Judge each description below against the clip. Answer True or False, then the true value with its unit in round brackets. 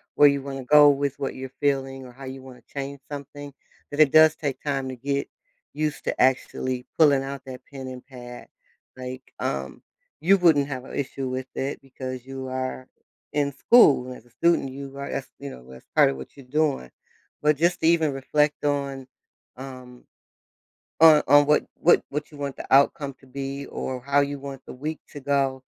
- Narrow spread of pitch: True (1.8 semitones)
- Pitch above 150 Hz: False (135 Hz)